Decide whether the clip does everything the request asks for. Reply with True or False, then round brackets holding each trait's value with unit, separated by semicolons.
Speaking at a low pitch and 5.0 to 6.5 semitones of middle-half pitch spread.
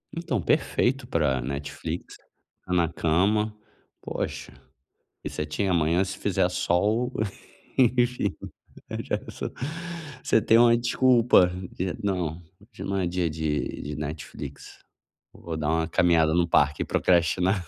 True (90 Hz; 5.4 semitones)